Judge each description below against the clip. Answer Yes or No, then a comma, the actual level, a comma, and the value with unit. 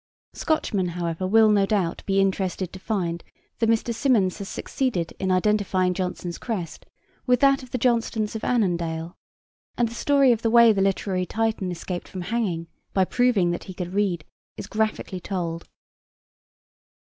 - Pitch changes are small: No, average, 3.9 semitones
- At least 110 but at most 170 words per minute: Yes, average, 160 wpm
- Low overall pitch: No, high, 195 Hz